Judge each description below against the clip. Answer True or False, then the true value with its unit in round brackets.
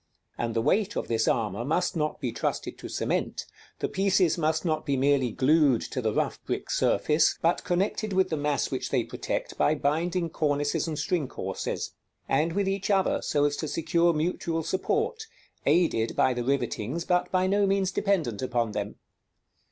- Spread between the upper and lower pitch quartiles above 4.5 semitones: True (5.1 semitones)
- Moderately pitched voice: True (160 Hz)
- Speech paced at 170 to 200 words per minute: True (180 wpm)